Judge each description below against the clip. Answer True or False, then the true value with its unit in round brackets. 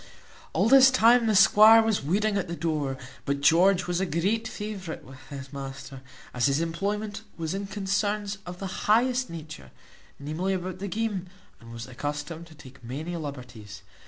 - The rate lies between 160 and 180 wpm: True (170 wpm)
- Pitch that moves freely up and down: True (6.3 semitones)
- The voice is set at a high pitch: False (175 Hz)